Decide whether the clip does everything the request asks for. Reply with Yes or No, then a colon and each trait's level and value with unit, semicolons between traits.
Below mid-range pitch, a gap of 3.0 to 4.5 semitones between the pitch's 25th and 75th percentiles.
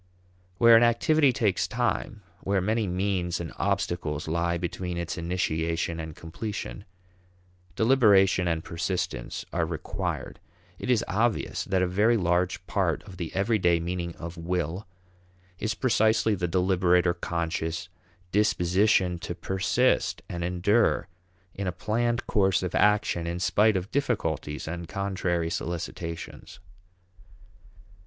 Yes: very low, 90 Hz; average, 3.5 semitones